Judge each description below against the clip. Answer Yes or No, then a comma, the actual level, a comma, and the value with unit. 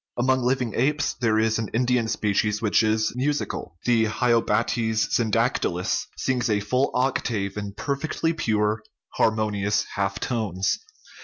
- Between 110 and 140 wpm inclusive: Yes, slow, 135 wpm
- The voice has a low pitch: Yes, low, 110 Hz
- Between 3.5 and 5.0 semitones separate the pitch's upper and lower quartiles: No, average, 3.1 semitones